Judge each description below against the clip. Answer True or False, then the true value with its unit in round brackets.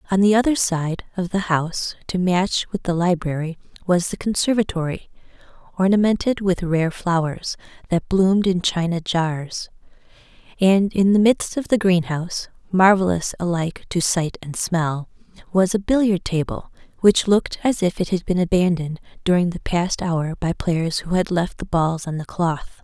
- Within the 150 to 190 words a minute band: True (165 wpm)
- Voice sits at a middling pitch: True (180 Hz)